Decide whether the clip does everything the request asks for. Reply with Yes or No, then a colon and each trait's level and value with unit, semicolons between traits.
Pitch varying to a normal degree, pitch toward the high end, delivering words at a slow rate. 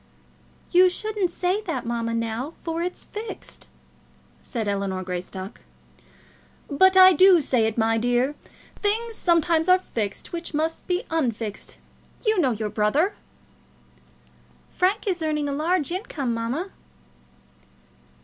No: wide, 8.1 semitones; very high, 310 Hz; slow, 125 wpm